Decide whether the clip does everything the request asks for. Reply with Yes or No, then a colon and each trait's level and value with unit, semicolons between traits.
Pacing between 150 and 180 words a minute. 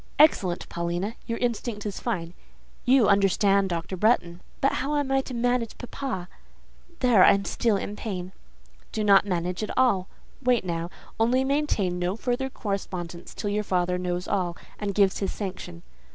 Yes: average, 165 wpm